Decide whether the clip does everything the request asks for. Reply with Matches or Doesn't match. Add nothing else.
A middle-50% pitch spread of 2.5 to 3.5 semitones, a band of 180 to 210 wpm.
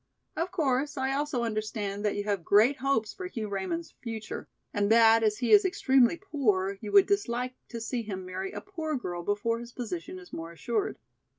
Doesn't match